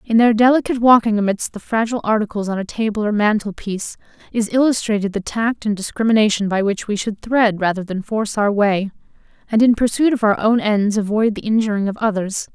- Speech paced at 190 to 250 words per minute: Yes, average, 200 wpm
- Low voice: No, high, 215 Hz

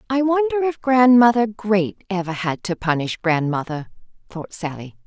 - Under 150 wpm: Yes, average, 140 wpm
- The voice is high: Yes, high, 205 Hz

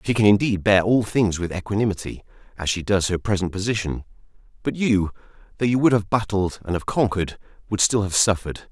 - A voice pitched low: Yes, low, 100 Hz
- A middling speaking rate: Yes, average, 185 wpm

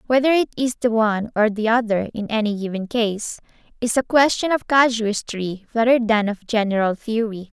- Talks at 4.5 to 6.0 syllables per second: Yes, 5.1 syllables/s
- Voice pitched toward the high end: Yes, high, 225 Hz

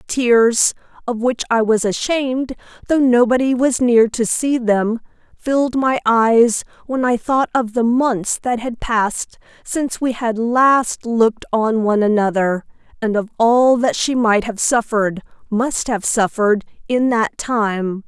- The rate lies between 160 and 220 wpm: No, average, 150 wpm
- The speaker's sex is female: Yes, female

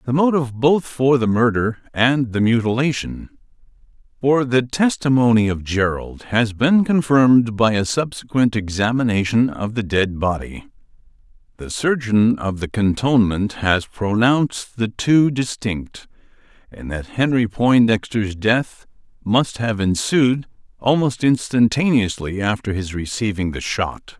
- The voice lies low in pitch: Yes, low, 115 Hz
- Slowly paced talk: Yes, slow, 125 wpm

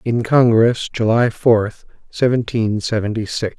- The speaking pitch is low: Yes, low, 115 Hz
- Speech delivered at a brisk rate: No, slow, 115 wpm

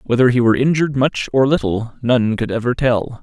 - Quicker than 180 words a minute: Yes, fast, 205 wpm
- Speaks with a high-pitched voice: No, low, 125 Hz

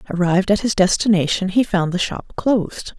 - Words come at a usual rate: Yes, average, 180 wpm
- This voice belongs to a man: No, female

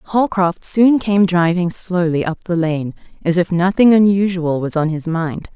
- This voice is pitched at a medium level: Yes, medium, 180 Hz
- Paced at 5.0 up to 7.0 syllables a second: No, 4.2 syllables/s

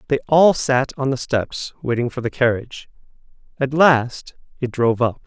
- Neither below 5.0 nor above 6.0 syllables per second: No, 4.8 syllables/s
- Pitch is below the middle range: Yes, low, 130 Hz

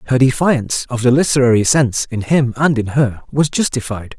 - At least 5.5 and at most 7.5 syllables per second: Yes, 5.6 syllables/s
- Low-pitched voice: Yes, low, 130 Hz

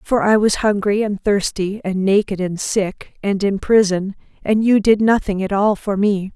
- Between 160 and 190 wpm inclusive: No, average, 200 wpm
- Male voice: No, female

